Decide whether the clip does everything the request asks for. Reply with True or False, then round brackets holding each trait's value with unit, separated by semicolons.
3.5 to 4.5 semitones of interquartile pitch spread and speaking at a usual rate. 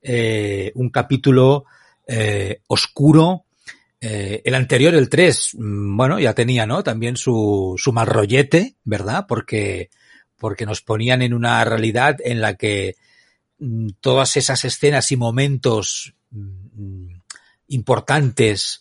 False (3.8 semitones; 110 wpm)